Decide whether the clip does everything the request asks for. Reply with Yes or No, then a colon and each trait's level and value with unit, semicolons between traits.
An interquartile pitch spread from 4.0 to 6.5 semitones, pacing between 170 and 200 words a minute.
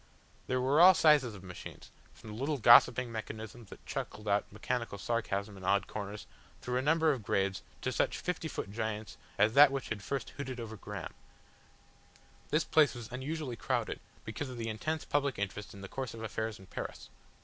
Yes: average, 4.5 semitones; average, 190 wpm